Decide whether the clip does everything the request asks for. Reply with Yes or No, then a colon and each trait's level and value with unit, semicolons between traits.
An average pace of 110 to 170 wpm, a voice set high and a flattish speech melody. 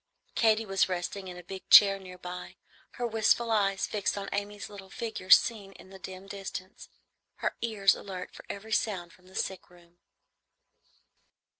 Yes: average, 165 wpm; high, 195 Hz; narrow, 2.0 semitones